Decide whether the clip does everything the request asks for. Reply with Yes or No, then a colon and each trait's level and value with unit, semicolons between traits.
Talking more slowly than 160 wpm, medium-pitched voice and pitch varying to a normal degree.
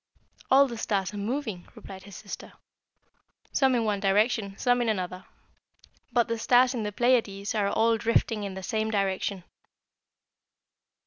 No: average, 150 wpm; high, 215 Hz; average, 3.3 semitones